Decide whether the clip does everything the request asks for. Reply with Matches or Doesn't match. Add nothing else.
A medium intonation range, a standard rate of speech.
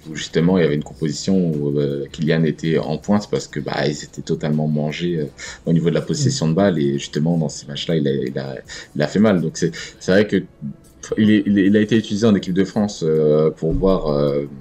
Doesn't match